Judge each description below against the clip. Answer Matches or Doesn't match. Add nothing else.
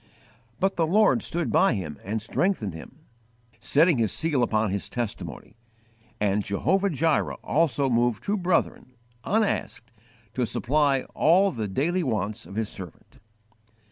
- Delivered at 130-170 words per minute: Matches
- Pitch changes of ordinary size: Doesn't match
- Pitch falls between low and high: Doesn't match